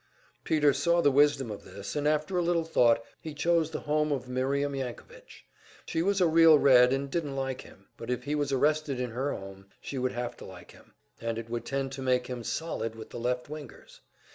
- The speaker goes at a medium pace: No, fast, 220 wpm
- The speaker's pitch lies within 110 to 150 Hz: Yes, low, 135 Hz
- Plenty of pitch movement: No, average, 3.7 semitones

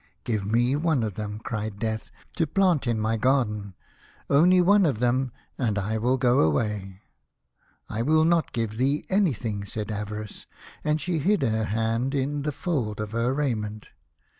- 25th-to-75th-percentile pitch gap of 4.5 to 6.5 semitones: Yes, average, 5.2 semitones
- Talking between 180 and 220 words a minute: Yes, average, 185 wpm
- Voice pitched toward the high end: No, low, 115 Hz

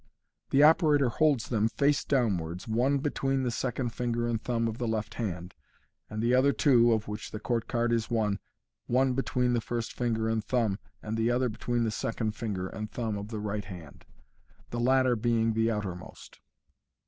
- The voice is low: Yes, low, 115 Hz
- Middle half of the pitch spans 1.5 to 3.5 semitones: Yes, narrow, 2.6 semitones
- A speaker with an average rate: Yes, average, 185 wpm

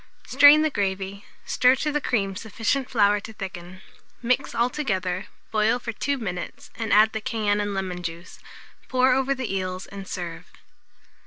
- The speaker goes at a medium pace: Yes, average, 160 wpm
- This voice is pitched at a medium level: No, high, 210 Hz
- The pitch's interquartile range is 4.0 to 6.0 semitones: Yes, average, 4.7 semitones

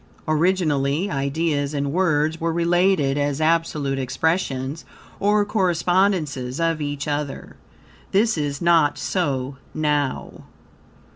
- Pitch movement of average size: Yes, average, 3.4 semitones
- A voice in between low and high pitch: Yes, medium, 155 Hz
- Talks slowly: Yes, slow, 100 wpm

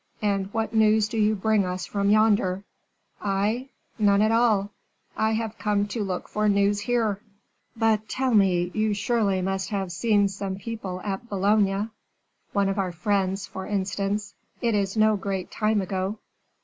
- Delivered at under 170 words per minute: Yes, average, 160 wpm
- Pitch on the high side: Yes, high, 205 Hz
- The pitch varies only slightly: Yes, narrow, 2.0 semitones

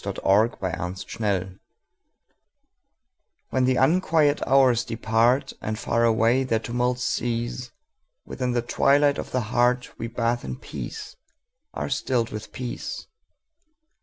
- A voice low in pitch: Yes, low, 120 Hz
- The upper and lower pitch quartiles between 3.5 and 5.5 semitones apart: No, narrow, 2.6 semitones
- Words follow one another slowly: Yes, slow, 110 wpm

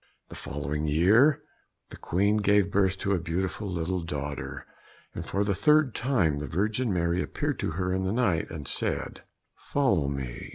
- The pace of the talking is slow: No, average, 170 wpm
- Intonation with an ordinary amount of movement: Yes, average, 4.3 semitones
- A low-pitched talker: Yes, very low, 95 Hz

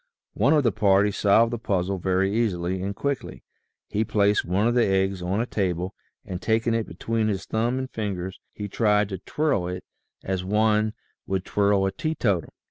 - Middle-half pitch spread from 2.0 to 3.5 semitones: Yes, average, 2.8 semitones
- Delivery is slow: No, average, 185 wpm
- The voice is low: Yes, low, 100 Hz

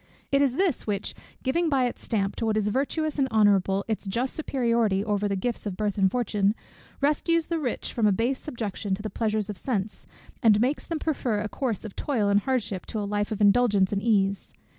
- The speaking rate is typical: No, fast, 215 wpm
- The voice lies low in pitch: No, high, 220 Hz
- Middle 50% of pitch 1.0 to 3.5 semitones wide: No, average, 4.3 semitones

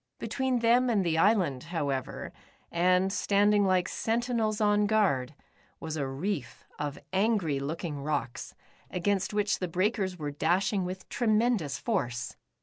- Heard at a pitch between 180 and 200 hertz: Yes, medium, 185 Hz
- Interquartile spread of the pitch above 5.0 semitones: Yes, wide, 5.4 semitones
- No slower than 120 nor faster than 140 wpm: Yes, slow, 135 wpm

